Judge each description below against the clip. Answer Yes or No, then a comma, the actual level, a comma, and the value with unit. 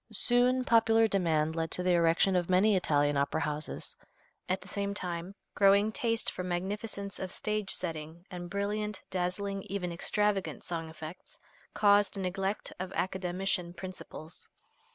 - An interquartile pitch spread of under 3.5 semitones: Yes, average, 2.8 semitones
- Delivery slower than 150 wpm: Yes, average, 140 wpm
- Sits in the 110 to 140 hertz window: No, medium, 185 Hz